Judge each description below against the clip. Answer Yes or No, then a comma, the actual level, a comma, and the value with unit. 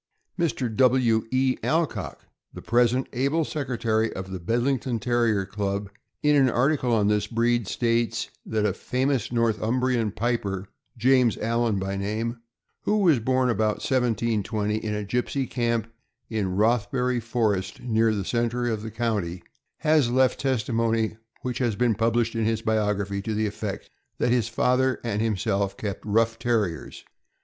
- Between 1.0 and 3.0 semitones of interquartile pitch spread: Yes, average, 2.7 semitones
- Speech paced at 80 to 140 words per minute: No, average, 150 wpm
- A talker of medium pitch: No, low, 115 Hz